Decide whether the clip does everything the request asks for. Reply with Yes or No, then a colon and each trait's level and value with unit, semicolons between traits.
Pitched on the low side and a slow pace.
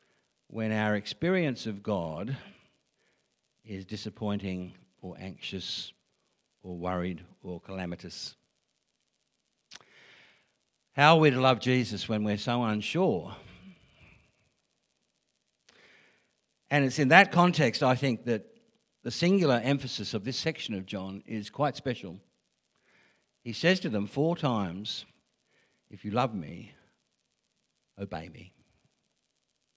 Yes: low, 115 Hz; slow, 110 wpm